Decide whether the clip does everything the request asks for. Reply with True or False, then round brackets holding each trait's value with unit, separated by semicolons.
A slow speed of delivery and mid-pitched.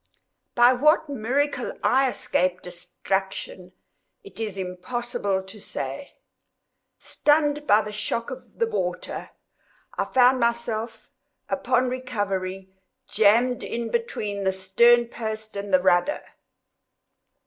False (105 wpm; 225 Hz)